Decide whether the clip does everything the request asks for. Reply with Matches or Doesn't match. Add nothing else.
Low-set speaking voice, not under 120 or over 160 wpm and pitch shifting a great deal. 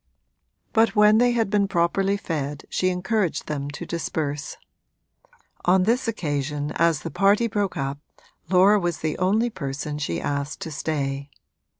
Doesn't match